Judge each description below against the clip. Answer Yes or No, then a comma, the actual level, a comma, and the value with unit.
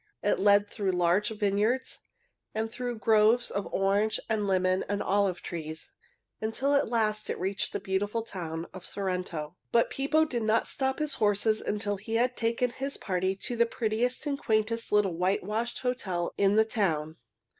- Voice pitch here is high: Yes, high, 210 Hz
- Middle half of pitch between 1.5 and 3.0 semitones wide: No, average, 3.4 semitones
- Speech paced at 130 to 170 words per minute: Yes, average, 165 wpm